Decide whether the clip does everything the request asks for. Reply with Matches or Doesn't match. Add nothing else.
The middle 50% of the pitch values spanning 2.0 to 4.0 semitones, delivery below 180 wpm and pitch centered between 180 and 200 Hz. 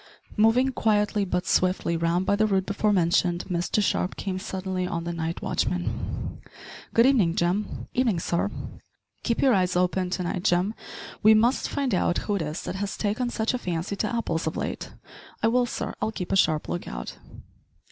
Doesn't match